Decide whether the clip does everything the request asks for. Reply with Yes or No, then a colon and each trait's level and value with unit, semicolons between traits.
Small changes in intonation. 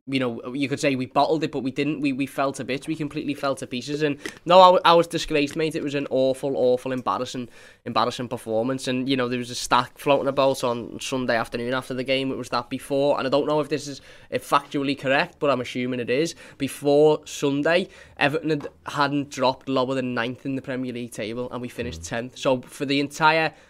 Yes: narrow, 2.3 semitones